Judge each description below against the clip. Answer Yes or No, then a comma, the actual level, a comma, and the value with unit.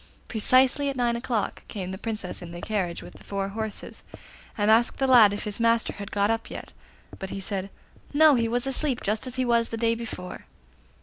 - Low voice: No, high, 225 Hz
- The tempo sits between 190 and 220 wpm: Yes, fast, 205 wpm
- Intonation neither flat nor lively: Yes, average, 3.3 semitones